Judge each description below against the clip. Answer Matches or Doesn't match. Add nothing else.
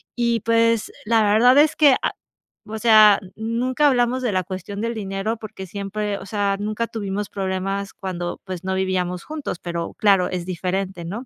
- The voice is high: Matches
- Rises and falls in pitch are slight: Doesn't match